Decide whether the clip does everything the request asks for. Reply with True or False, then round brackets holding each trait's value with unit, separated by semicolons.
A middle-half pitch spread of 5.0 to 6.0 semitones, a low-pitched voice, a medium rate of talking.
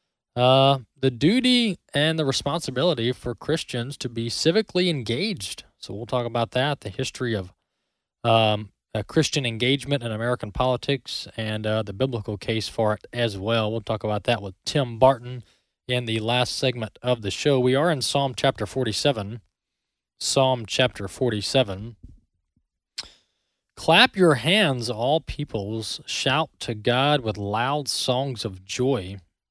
False (3.8 semitones; 125 Hz; 145 wpm)